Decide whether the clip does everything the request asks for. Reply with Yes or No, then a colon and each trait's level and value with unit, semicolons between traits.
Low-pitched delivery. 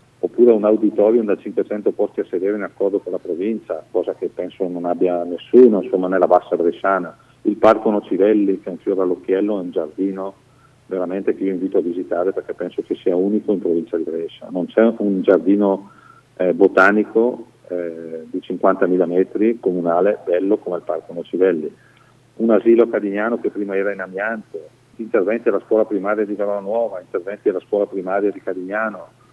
Yes: low, 100 Hz